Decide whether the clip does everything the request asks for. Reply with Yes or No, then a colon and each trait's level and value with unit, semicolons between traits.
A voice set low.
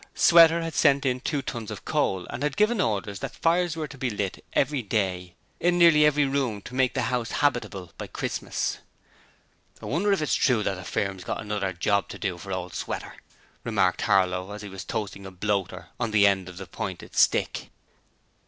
Yes: low, 110 Hz